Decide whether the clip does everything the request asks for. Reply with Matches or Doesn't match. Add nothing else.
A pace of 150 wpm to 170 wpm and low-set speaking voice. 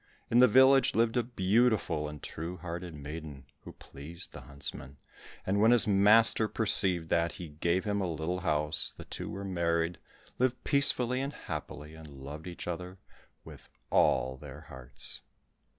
Matches